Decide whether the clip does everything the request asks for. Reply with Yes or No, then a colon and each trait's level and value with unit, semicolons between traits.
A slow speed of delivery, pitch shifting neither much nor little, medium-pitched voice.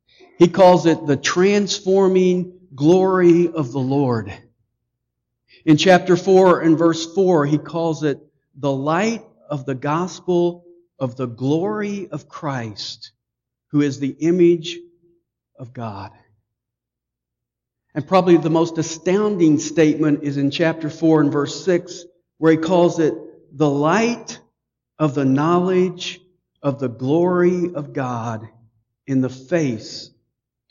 Yes: slow, 125 wpm; average, 4.5 semitones; medium, 155 Hz